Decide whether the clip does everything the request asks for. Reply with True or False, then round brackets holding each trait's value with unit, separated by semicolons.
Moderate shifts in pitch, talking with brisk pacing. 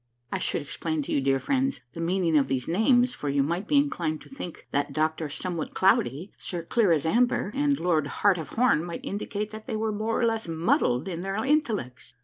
False (6.2 semitones; 215 wpm)